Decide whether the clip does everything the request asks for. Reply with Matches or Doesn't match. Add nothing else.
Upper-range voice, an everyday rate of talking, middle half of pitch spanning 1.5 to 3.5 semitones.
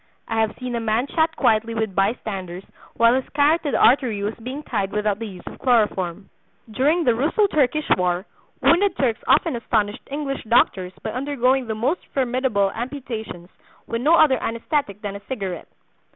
Doesn't match